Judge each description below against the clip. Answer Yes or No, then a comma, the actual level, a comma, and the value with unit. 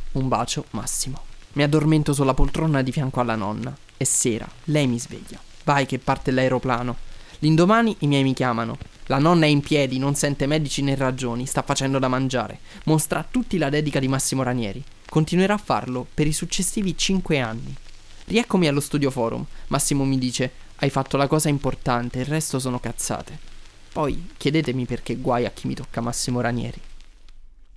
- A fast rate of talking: Yes, fast, 175 wpm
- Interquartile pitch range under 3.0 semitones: No, average, 3.6 semitones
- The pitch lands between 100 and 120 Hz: No, low, 135 Hz